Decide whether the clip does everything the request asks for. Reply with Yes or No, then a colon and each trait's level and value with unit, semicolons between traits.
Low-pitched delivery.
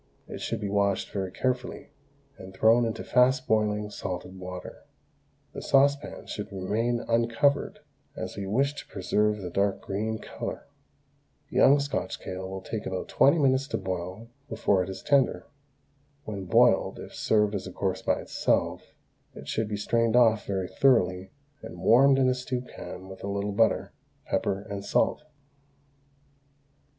Yes: low, 105 Hz